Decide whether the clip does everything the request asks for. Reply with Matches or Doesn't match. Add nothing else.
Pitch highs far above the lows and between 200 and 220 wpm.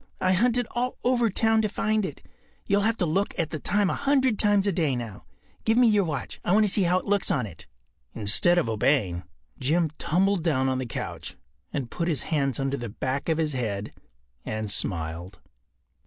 Matches